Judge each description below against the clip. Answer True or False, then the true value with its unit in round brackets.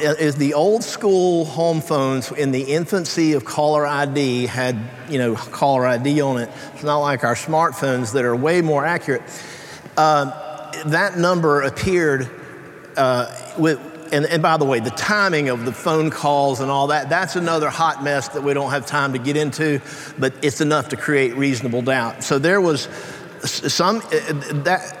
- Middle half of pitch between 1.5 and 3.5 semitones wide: True (2.9 semitones)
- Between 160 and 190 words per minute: True (180 wpm)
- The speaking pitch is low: False (145 Hz)